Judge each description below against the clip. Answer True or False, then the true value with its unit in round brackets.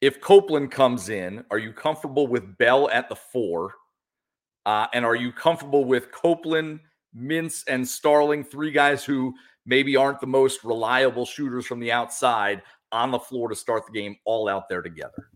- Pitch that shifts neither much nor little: True (3.6 semitones)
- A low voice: True (130 Hz)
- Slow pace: False (175 wpm)